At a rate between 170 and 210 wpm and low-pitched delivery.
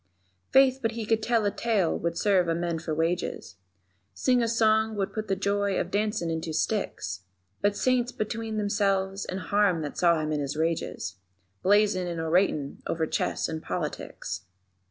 No: average, 180 wpm; high, 195 Hz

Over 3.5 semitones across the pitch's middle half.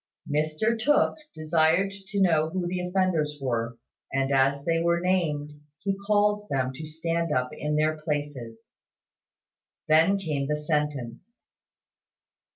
Yes: average, 4.0 semitones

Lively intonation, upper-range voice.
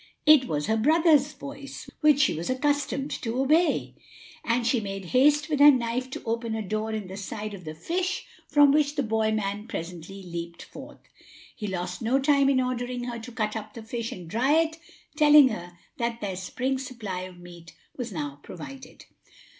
Yes: wide, 5.9 semitones; high, 235 Hz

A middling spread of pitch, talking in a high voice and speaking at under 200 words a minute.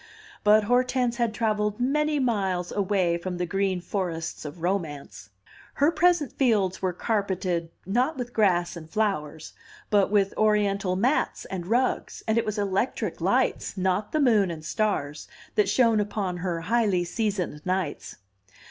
Yes: average, 4.2 semitones; high, 200 Hz; average, 150 wpm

